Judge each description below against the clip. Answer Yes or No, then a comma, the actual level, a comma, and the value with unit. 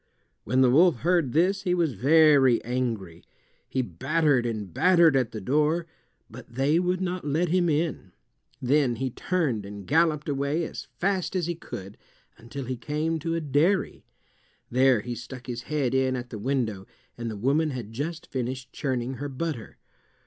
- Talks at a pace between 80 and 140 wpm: No, average, 170 wpm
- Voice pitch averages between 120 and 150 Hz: Yes, low, 135 Hz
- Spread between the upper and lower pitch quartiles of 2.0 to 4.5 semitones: No, average, 5.0 semitones